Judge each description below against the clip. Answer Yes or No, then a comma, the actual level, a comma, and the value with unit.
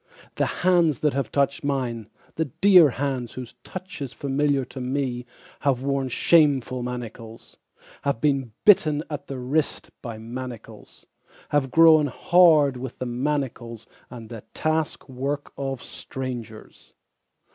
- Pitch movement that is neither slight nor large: Yes, average, 3.0 semitones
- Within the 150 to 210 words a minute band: No, slow, 135 wpm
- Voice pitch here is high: No, low, 135 Hz